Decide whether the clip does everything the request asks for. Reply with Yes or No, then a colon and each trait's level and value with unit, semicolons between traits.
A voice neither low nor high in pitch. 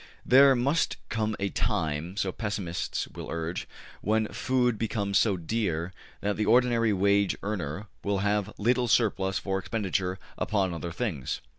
No: low, 100 Hz